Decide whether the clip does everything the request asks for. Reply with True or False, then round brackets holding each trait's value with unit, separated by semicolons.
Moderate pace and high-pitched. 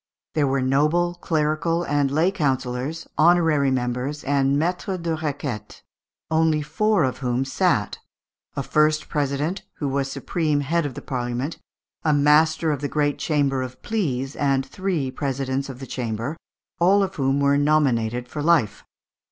False (150 wpm; 145 Hz)